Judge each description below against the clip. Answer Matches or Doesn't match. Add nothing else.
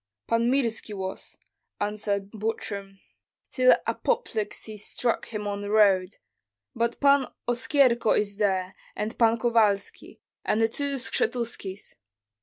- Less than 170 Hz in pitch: Doesn't match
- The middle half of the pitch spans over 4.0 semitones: Doesn't match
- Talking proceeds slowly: Matches